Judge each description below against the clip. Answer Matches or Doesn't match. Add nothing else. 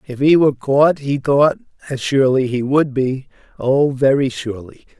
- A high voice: Doesn't match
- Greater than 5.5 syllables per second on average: Doesn't match